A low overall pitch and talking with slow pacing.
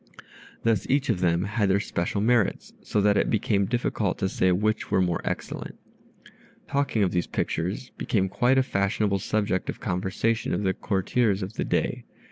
No: low, 100 Hz; average, 175 wpm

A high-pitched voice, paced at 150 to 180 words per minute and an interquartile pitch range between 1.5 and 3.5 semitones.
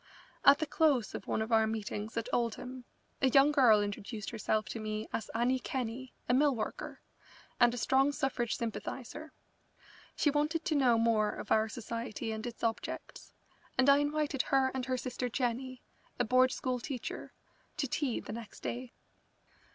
Yes: high, 245 Hz; average, 170 wpm; average, 3.1 semitones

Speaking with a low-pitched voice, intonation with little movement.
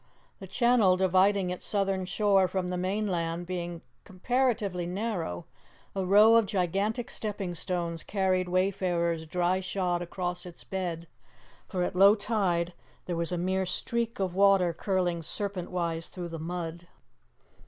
No: medium, 185 Hz; narrow, 2.1 semitones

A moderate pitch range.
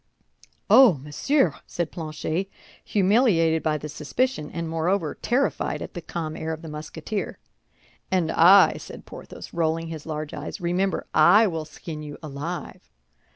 Yes: average, 3.5 semitones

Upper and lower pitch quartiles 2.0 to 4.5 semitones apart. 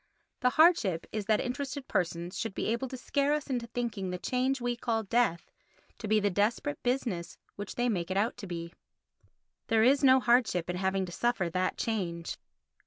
No: average, 5.1 semitones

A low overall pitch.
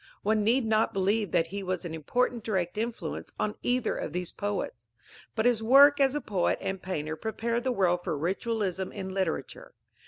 No: high, 205 Hz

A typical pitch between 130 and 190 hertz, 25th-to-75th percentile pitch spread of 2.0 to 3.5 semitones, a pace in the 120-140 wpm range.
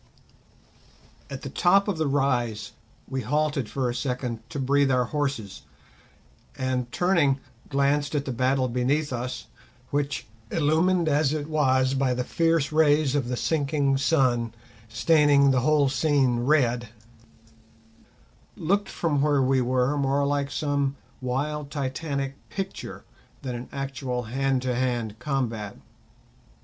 Yes: low, 135 Hz; average, 2.7 semitones; slow, 135 wpm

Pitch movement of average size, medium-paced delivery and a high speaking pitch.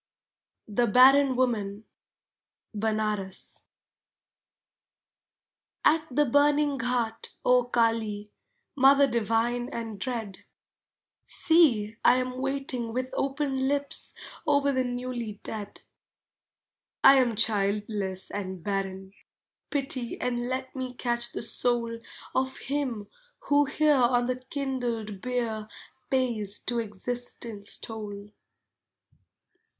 No: average, 3.6 semitones; slow, 100 wpm; high, 240 Hz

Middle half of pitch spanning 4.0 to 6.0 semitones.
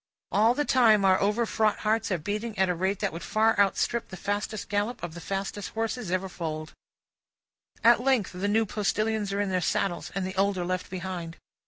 No: average, 2.9 semitones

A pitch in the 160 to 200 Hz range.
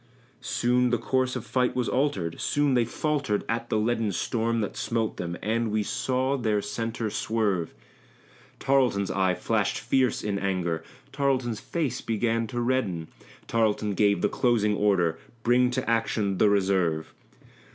No: low, 115 Hz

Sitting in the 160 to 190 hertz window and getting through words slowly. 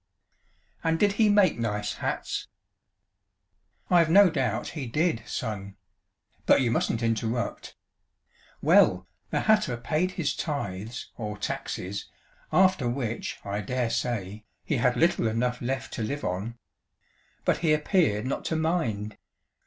No: low, 125 Hz; slow, 130 wpm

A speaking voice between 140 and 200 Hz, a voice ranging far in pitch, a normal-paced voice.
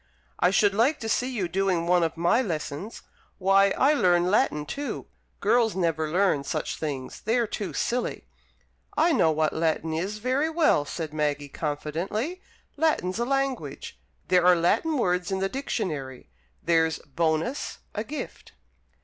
Yes: medium, 185 Hz; wide, 6.8 semitones; average, 150 wpm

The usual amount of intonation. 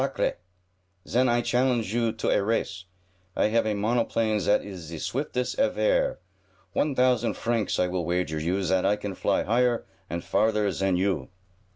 Yes: average, 4.3 semitones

